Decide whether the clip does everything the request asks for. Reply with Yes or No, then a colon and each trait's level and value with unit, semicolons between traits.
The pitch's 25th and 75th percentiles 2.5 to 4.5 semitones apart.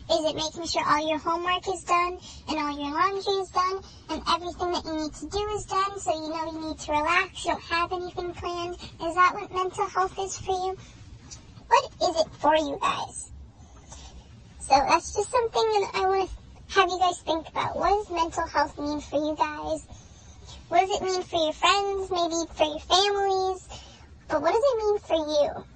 Yes: average, 3.1 semitones